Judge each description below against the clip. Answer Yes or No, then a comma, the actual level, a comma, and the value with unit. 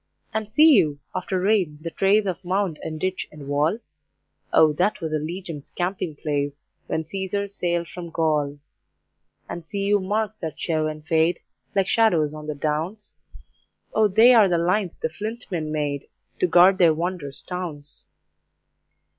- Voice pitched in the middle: Yes, medium, 175 Hz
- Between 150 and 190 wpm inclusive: Yes, average, 165 wpm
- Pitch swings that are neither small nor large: Yes, average, 4.3 semitones